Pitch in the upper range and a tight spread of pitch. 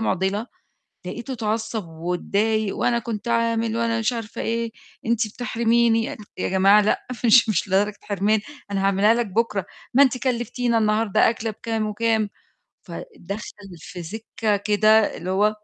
Yes: high, 220 Hz; narrow, 2.2 semitones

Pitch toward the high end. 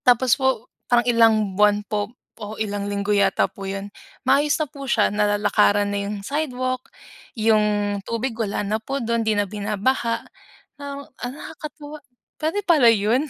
Yes: high, 225 Hz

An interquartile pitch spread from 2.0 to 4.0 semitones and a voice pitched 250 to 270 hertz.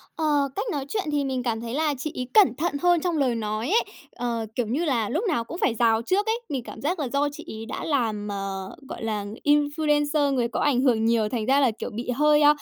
No: average, 4.7 semitones; very high, 265 Hz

